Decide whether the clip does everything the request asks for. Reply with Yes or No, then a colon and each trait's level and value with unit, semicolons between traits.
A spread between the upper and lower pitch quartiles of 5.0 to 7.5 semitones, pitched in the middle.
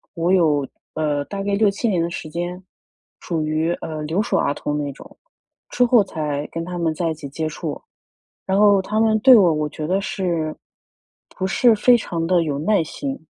No: average, 4.3 semitones; medium, 170 Hz